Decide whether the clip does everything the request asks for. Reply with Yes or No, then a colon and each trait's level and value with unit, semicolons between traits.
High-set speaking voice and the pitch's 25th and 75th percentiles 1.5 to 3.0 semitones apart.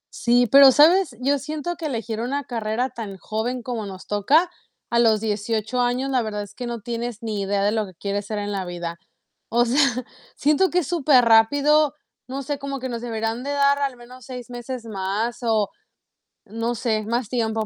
No: high, 235 Hz; average, 3.6 semitones